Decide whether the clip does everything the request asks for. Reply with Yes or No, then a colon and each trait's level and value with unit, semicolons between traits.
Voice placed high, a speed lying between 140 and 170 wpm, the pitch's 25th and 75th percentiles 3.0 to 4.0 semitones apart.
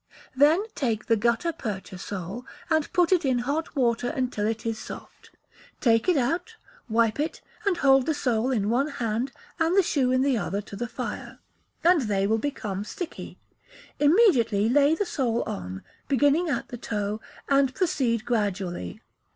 No: high, 245 Hz; average, 165 wpm; average, 5.1 semitones